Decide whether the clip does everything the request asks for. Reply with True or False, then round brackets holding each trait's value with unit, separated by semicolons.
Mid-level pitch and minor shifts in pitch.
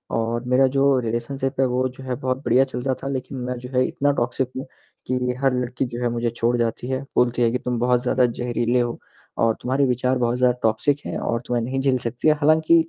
False (125 Hz; 1.6 semitones)